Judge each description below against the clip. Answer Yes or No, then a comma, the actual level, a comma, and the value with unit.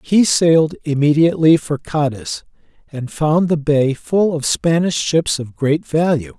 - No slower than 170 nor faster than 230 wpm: No, average, 150 wpm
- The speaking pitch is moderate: Yes, medium, 155 Hz